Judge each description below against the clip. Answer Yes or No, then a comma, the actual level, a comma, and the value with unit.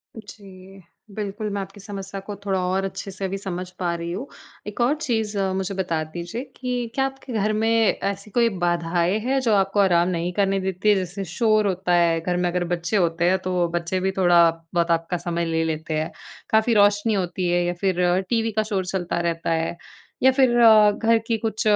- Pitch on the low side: No, high, 190 Hz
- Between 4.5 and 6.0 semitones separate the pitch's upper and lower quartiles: No, average, 3.5 semitones